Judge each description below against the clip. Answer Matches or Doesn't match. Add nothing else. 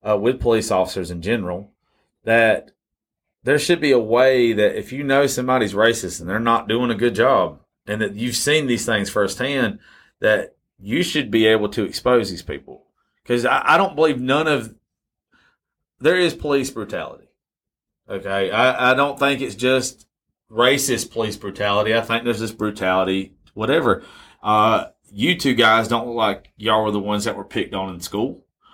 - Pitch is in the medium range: Doesn't match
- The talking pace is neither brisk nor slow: Matches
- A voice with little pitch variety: Doesn't match